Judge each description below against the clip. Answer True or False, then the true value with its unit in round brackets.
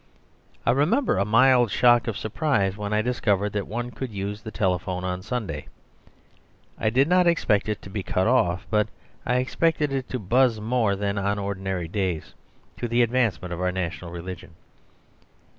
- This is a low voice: True (105 Hz)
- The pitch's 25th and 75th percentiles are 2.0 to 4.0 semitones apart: False (4.5 semitones)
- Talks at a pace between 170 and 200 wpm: True (175 wpm)